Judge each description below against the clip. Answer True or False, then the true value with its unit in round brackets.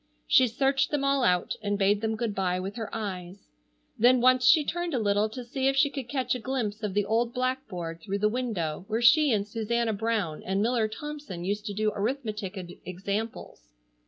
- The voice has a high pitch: True (220 Hz)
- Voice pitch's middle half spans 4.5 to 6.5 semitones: False (4.1 semitones)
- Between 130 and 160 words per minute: False (200 wpm)